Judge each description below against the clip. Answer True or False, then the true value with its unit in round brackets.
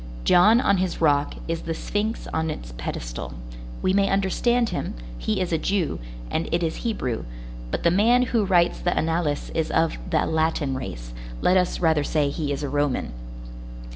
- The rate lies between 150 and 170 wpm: False (180 wpm)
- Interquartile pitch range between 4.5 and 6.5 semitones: True (4.9 semitones)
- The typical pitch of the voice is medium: True (165 Hz)